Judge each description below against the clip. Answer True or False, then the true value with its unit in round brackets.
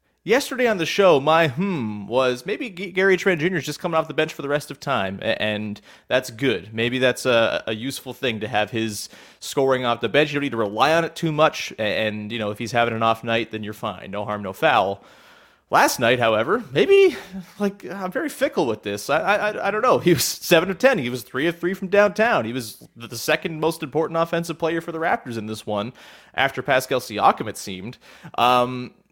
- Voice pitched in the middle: True (145 Hz)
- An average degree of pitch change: False (7.4 semitones)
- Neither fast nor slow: False (225 wpm)